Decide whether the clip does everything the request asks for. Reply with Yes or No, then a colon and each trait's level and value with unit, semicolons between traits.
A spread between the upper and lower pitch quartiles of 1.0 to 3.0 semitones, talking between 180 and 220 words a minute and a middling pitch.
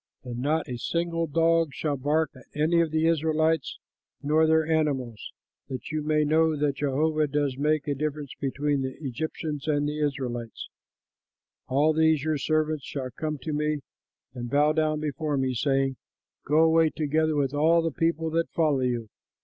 No: narrow, 2.4 semitones; average, 165 wpm; medium, 150 Hz